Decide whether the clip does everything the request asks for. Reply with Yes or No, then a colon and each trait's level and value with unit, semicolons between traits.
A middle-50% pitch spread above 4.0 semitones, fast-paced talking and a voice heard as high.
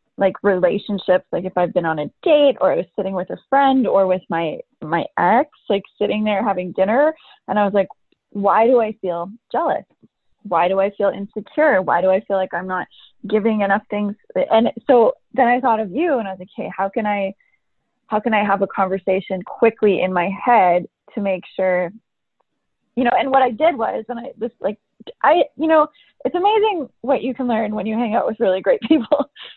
Yes: average, 4.6 semitones; fast, 215 wpm; high, 210 Hz